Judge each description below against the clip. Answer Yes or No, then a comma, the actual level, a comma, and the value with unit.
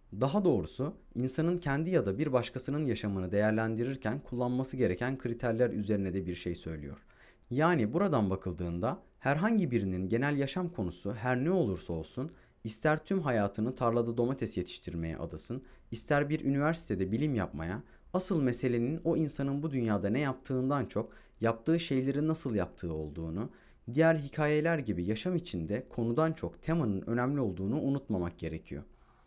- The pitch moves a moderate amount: No, wide, 6.0 semitones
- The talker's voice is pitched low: Yes, low, 120 Hz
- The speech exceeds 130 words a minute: Yes, fast, 140 wpm